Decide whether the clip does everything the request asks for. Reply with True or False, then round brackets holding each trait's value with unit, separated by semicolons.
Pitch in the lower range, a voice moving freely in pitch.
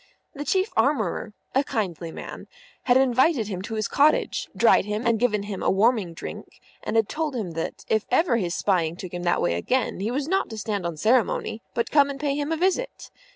False (225 Hz; 6.2 semitones)